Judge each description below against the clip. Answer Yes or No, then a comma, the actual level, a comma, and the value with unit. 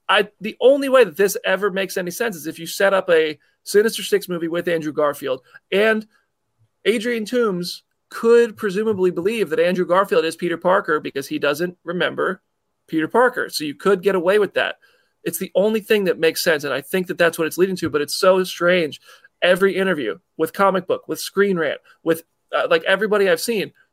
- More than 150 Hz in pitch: Yes, high, 190 Hz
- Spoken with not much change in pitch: No, average, 3.8 semitones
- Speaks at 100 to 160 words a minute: No, fast, 205 wpm